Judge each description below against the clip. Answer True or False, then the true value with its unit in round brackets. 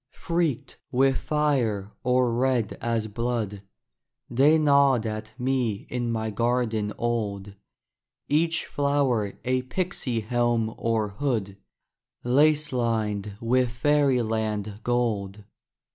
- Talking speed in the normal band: False (100 wpm)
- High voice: False (120 Hz)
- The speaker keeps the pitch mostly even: False (3.5 semitones)